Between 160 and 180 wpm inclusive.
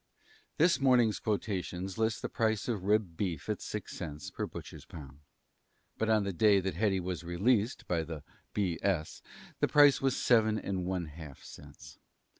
Yes: average, 170 wpm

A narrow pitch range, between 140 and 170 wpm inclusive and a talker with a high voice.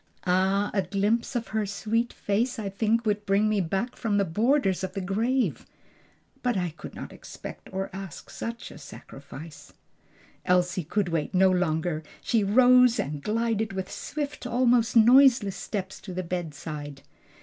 No: average, 4.1 semitones; average, 160 wpm; high, 200 Hz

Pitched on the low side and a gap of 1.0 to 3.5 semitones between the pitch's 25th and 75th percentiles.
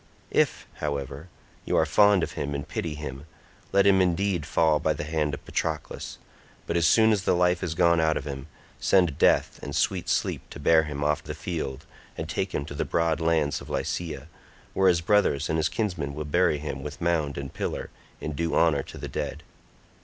Yes: very low, 80 Hz; average, 3.2 semitones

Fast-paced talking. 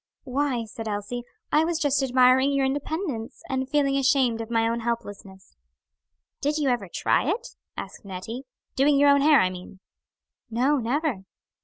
No: average, 160 wpm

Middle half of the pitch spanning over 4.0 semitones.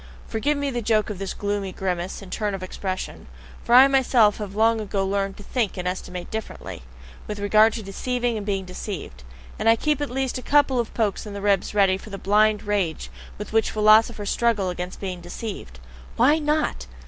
No: average, 3.1 semitones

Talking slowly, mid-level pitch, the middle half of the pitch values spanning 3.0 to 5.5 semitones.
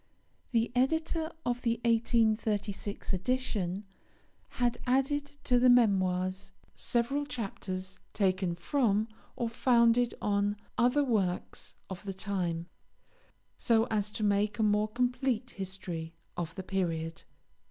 No: slow, 115 wpm; high, 215 Hz; average, 4.3 semitones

